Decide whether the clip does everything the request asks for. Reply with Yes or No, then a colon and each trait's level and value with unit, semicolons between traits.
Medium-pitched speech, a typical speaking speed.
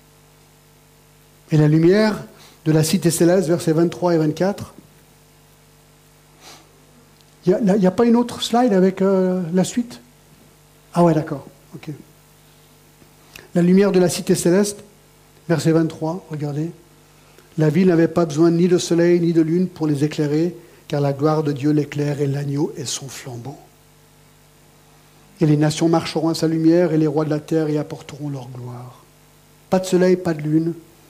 Yes: medium, 160 Hz; average, 160 wpm